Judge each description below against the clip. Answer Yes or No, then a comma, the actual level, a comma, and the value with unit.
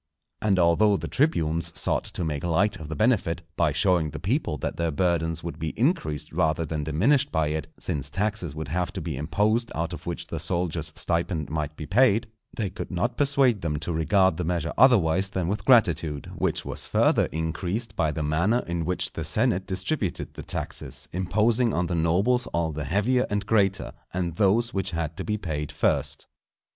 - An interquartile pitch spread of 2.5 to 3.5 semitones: No, average, 4.7 semitones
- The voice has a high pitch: No, very low, 85 Hz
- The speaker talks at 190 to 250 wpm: Yes, average, 195 wpm